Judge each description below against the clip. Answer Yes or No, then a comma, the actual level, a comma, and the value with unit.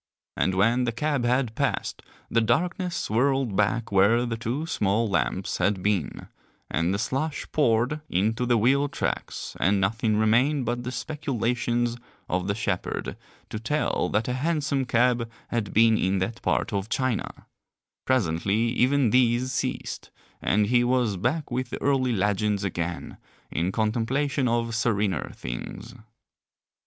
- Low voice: Yes, low, 115 Hz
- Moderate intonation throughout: Yes, average, 3.8 semitones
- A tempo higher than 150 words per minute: No, average, 145 wpm